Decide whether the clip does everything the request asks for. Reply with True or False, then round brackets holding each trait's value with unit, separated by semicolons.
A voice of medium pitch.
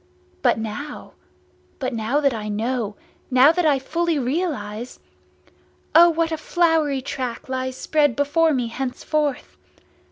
False (270 Hz)